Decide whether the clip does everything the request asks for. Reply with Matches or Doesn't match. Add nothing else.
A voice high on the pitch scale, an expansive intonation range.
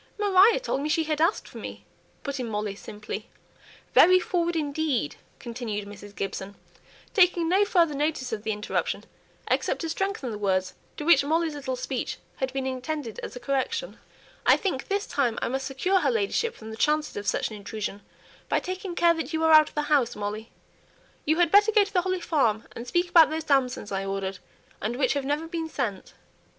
Matches